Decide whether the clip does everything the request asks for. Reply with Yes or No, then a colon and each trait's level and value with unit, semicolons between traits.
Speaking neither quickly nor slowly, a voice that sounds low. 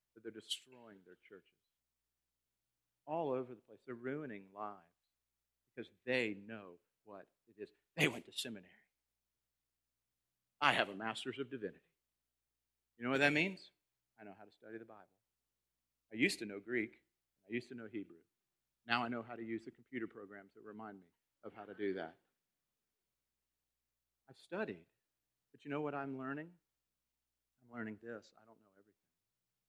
Yes: average, 165 wpm; very low, 95 Hz